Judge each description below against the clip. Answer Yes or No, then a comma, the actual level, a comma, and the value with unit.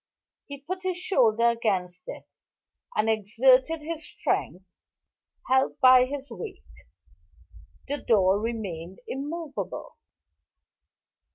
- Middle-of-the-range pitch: No, very high, 255 Hz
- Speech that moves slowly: Yes, slow, 95 wpm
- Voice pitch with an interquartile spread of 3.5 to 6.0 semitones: Yes, wide, 5.5 semitones